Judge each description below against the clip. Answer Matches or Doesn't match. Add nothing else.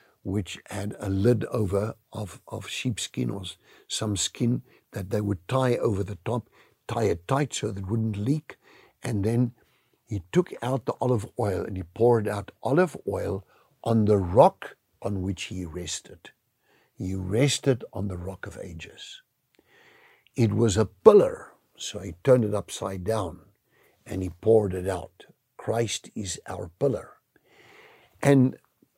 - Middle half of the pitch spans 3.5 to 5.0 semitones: Matches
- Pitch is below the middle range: Matches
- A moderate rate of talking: Matches